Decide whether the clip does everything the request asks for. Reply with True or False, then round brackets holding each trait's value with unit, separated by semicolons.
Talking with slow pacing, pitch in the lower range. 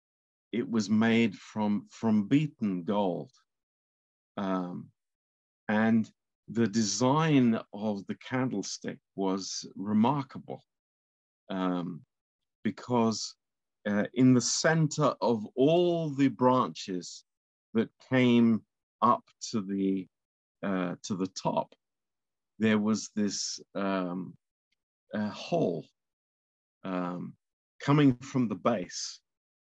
True (95 wpm; 105 Hz)